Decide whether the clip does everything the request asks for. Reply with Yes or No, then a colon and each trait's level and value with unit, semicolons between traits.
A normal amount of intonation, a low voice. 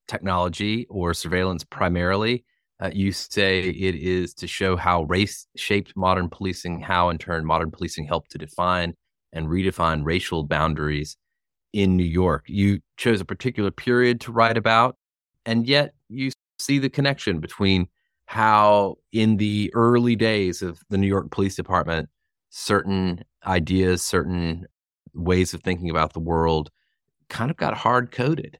Yes: average, 3.8 semitones; very low, 95 Hz